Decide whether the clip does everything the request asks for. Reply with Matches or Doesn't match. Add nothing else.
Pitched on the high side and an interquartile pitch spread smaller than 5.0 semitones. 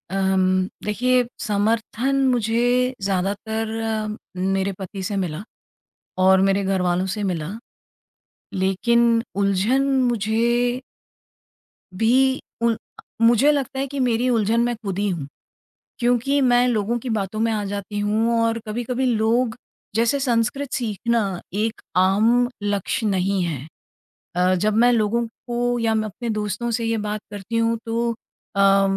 Matches